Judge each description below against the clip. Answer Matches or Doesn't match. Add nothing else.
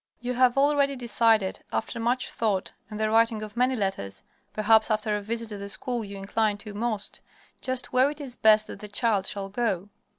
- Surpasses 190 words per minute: Matches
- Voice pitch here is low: Doesn't match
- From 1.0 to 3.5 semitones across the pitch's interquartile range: Matches